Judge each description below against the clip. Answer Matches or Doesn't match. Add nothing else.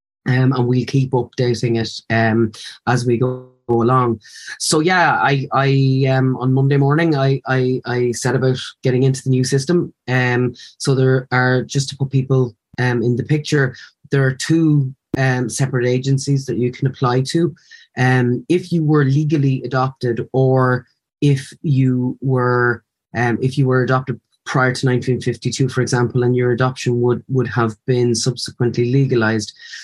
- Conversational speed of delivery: Matches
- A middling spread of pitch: Doesn't match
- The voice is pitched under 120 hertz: Doesn't match